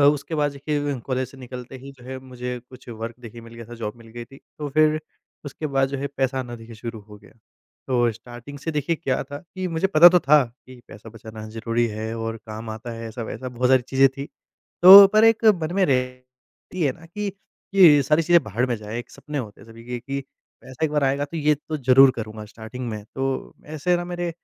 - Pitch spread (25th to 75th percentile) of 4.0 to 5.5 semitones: Yes, average, 4.3 semitones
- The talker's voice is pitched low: Yes, low, 130 Hz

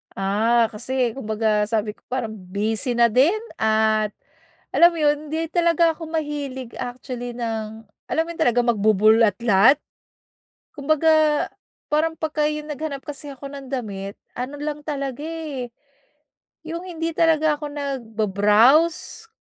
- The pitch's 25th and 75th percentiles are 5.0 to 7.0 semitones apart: Yes, wide, 5.5 semitones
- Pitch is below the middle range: No, very high, 265 Hz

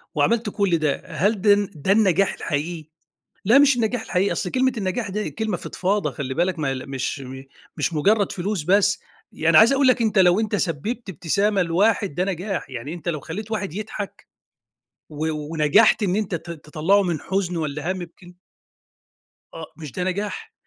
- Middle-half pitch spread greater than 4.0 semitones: Yes, average, 4.7 semitones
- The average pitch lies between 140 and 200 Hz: Yes, medium, 185 Hz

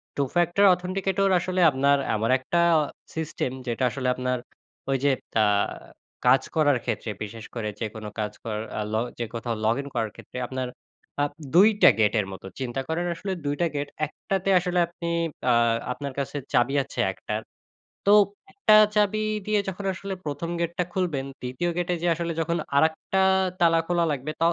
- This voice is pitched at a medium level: Yes, medium, 145 Hz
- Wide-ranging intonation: Yes, wide, 5.9 semitones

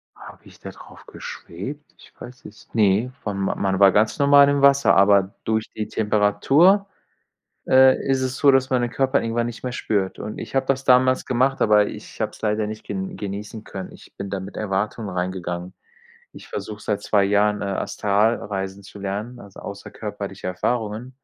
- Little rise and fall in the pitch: No, average, 4.3 semitones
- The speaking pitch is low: Yes, low, 105 Hz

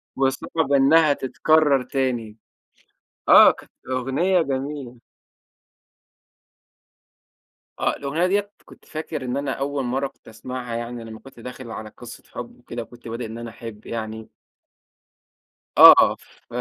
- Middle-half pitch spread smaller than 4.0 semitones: Yes, average, 3.2 semitones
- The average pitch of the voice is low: Yes, low, 130 Hz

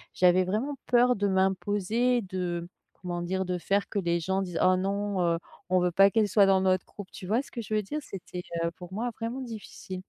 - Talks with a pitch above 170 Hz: Yes, high, 190 Hz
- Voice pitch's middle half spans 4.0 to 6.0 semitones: No, average, 2.8 semitones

